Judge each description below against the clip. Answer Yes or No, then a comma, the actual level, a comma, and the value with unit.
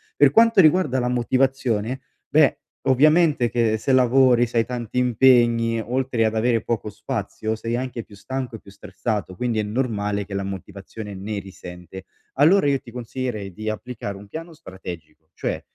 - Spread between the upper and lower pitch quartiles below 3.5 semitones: No, average, 4.1 semitones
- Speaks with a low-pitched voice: Yes, low, 115 Hz